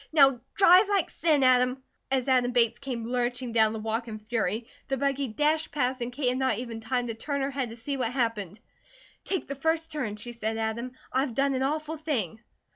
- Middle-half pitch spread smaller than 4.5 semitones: Yes, average, 3.4 semitones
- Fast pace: Yes, fast, 215 wpm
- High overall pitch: Yes, very high, 250 Hz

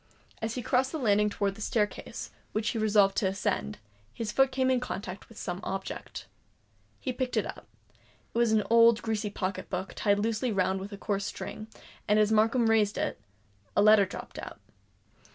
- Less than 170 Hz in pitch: No, high, 215 Hz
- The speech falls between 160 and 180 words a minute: No, average, 190 wpm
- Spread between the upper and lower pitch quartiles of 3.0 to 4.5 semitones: No, narrow, 2.4 semitones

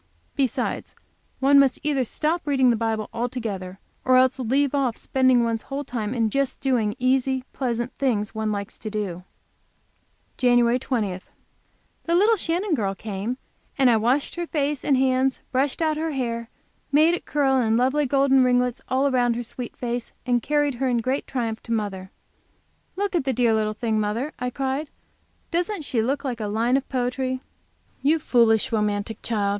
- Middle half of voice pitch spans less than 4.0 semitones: Yes, average, 3.4 semitones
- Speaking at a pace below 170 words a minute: No, average, 175 wpm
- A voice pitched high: Yes, very high, 250 Hz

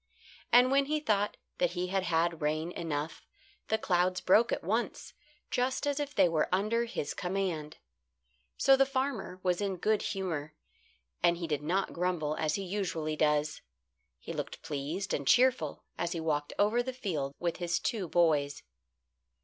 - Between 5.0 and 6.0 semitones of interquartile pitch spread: Yes, average, 5.3 semitones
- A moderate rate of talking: Yes, average, 165 wpm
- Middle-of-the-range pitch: Yes, medium, 180 Hz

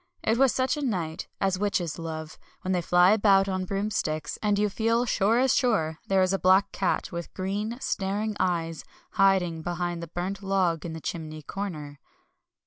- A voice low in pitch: No, high, 190 Hz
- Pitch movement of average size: Yes, average, 3.4 semitones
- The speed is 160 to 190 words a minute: Yes, average, 180 wpm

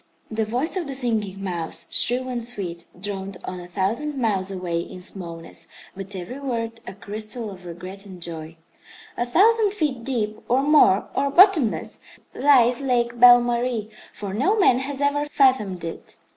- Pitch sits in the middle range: No, high, 230 Hz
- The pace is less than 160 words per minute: No, average, 165 wpm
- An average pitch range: No, wide, 5.7 semitones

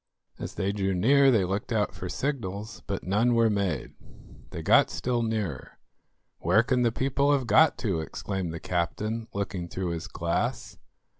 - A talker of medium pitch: No, low, 105 Hz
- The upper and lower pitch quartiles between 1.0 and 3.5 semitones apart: No, average, 4.4 semitones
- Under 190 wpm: Yes, average, 165 wpm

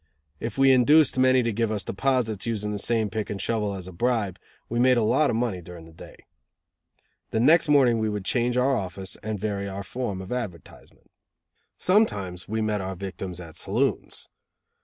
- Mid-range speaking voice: No, low, 110 Hz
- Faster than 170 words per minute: Yes, average, 190 wpm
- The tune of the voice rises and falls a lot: No, average, 4.3 semitones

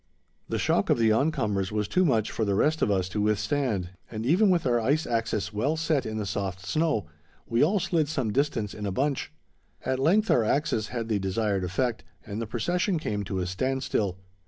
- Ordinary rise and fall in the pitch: No, wide, 6.1 semitones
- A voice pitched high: No, low, 115 Hz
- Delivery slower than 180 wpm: No, fast, 205 wpm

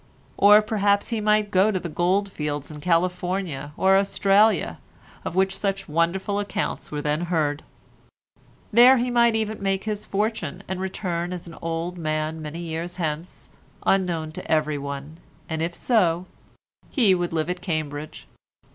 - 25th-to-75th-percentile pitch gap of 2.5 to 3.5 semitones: No, average, 4.1 semitones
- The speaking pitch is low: No, medium, 180 Hz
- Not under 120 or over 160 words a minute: Yes, average, 155 wpm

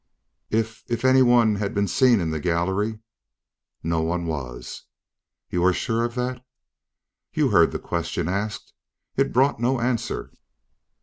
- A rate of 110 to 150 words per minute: Yes, average, 145 wpm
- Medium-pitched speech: No, low, 105 Hz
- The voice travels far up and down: Yes, wide, 5.8 semitones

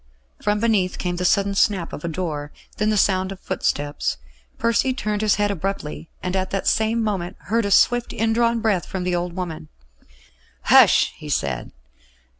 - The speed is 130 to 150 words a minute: No, average, 175 wpm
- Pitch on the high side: Yes, high, 195 Hz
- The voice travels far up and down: No, average, 3.4 semitones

